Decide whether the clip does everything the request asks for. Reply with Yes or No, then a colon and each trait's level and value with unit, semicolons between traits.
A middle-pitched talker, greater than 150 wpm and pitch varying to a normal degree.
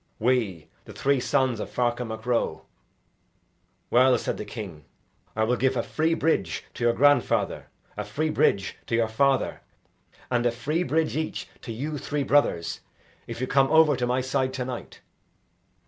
No: low, 125 Hz; average, 170 wpm; average, 3.5 semitones